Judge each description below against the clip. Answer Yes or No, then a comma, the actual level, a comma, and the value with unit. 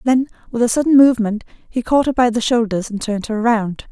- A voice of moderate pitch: No, high, 230 Hz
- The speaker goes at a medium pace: No, fast, 230 wpm